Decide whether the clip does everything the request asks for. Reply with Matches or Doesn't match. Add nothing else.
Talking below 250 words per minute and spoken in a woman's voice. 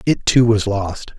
Doesn't match